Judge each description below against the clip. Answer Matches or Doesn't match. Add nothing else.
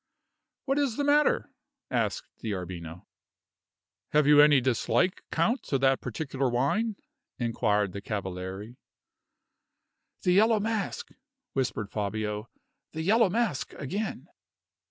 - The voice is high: Doesn't match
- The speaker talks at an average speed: Doesn't match